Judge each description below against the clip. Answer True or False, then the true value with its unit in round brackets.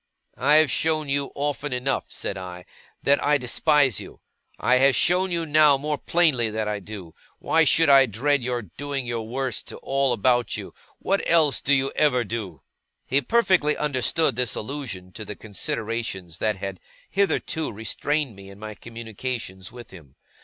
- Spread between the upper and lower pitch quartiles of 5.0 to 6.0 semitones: True (5.3 semitones)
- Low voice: True (125 Hz)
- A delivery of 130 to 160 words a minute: False (170 wpm)